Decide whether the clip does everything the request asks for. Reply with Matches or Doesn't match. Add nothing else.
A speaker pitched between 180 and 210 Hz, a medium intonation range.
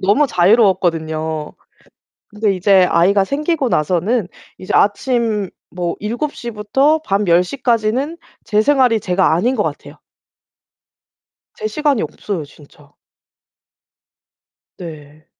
Doesn't match